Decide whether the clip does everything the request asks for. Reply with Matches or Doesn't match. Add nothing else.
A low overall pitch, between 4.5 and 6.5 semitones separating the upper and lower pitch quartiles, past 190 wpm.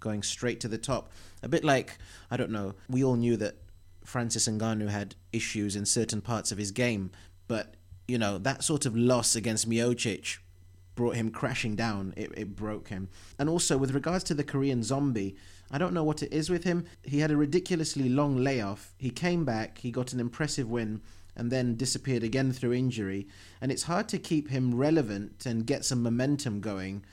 Matches